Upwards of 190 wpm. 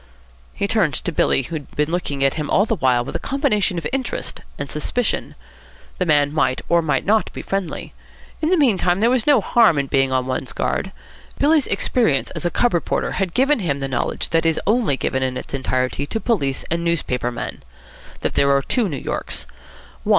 Yes: fast, 205 wpm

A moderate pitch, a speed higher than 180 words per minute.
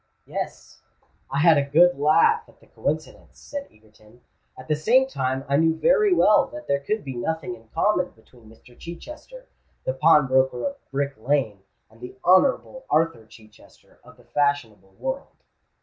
No: medium, 145 Hz; average, 165 wpm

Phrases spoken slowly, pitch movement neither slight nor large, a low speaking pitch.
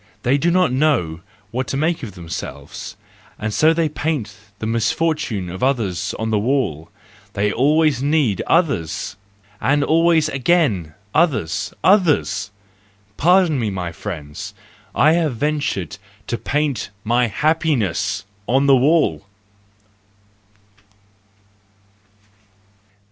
No: slow, 110 wpm; wide, 7.5 semitones; low, 130 Hz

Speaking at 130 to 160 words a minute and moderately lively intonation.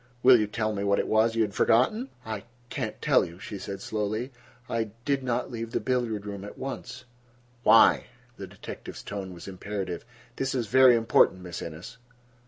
No: average, 190 wpm; average, 3.4 semitones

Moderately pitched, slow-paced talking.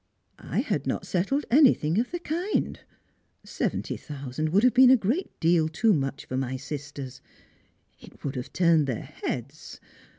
No: medium, 160 Hz; average, 165 wpm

